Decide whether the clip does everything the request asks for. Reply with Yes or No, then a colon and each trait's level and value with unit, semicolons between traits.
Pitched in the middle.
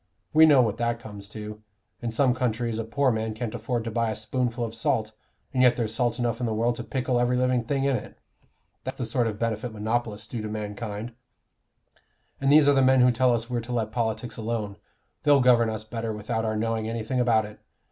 No: low, 115 Hz